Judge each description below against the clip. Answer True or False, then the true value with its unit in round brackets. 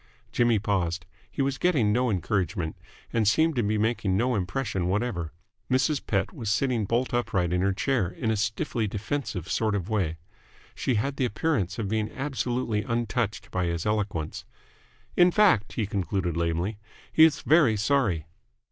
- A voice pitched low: True (110 Hz)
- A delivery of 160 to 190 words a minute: True (165 wpm)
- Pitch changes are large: False (4.9 semitones)